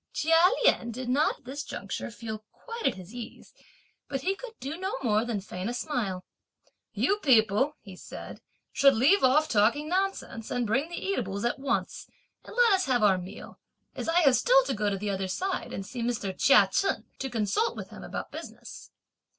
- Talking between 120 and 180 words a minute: No, average, 200 wpm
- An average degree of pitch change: No, wide, 7.6 semitones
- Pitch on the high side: Yes, very high, 250 Hz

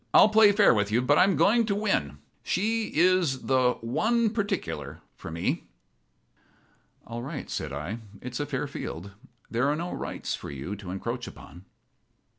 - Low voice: Yes, low, 130 Hz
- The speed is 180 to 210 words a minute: No, average, 170 wpm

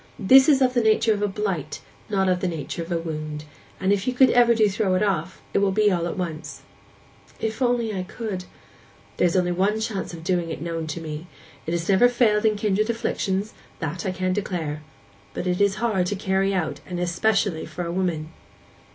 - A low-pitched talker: No, high, 190 Hz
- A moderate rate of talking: No, fast, 210 wpm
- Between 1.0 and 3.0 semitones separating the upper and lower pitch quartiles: No, average, 3.9 semitones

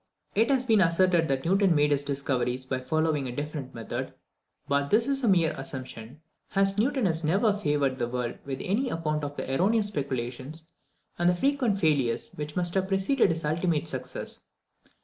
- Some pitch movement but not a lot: No, wide, 6.1 semitones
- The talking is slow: No, average, 180 wpm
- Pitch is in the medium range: Yes, medium, 160 Hz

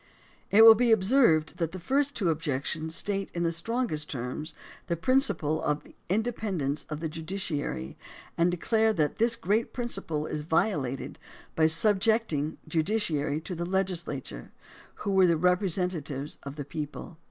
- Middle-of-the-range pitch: Yes, medium, 170 Hz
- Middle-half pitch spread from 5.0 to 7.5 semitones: Yes, wide, 5.5 semitones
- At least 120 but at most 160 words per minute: Yes, average, 155 wpm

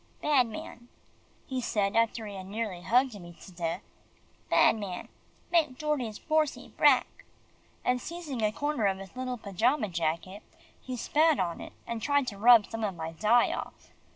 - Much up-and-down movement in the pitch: No, average, 4.8 semitones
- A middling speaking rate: Yes, average, 170 wpm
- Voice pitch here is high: Yes, high, 225 Hz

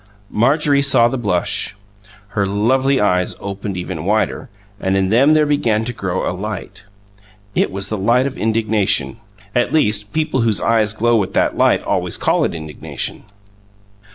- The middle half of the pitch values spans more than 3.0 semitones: Yes, average, 4.2 semitones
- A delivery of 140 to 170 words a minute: Yes, average, 160 wpm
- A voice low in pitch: Yes, low, 110 Hz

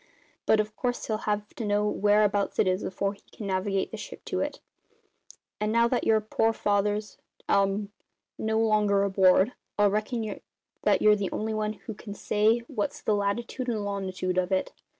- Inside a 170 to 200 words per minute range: Yes, average, 180 wpm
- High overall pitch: Yes, high, 210 Hz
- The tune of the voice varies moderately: No, narrow, 1.5 semitones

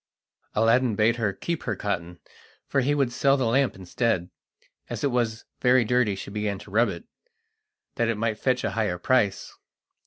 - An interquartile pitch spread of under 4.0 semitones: Yes, average, 3.5 semitones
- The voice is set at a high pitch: No, low, 115 Hz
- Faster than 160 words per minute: Yes, average, 180 wpm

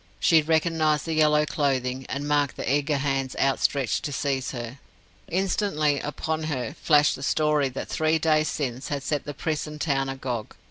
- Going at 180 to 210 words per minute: No, average, 170 wpm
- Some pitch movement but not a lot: No, narrow, 2.3 semitones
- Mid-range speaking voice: Yes, medium, 145 Hz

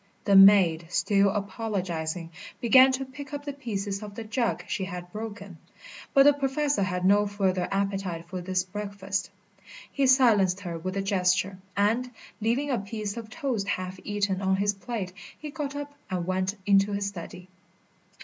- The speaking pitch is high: Yes, high, 200 Hz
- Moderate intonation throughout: Yes, average, 3.6 semitones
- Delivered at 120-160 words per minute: No, average, 170 wpm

